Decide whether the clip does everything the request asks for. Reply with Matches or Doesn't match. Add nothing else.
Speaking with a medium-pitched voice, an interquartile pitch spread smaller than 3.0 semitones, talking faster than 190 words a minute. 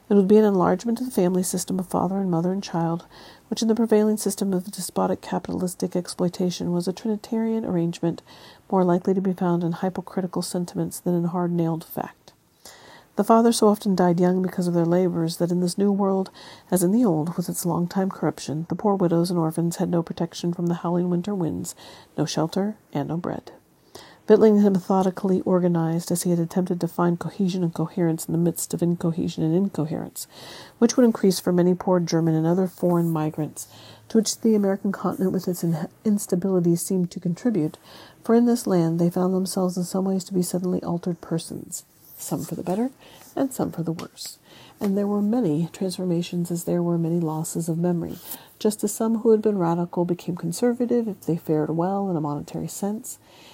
Matches